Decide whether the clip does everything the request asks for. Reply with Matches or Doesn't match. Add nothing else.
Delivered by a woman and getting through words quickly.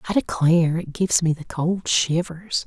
Doesn't match